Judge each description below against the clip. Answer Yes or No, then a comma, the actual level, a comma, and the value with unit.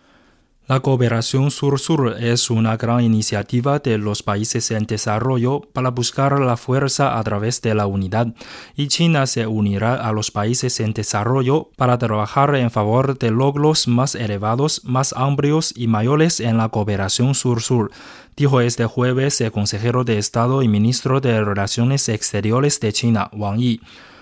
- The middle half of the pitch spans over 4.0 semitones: No, average, 3.4 semitones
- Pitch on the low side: Yes, low, 120 Hz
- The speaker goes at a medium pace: Yes, average, 155 wpm